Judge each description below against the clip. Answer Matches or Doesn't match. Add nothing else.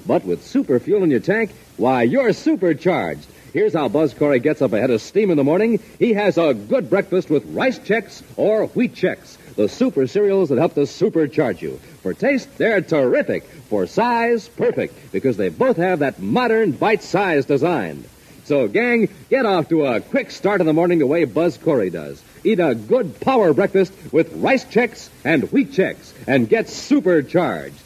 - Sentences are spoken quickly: Doesn't match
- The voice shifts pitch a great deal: Matches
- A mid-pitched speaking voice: Doesn't match